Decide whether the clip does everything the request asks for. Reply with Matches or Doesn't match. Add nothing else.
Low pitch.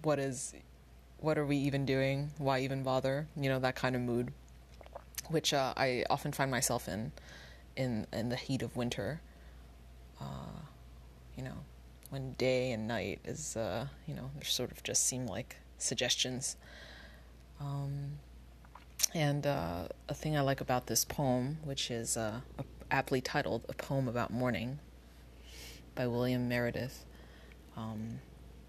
Matches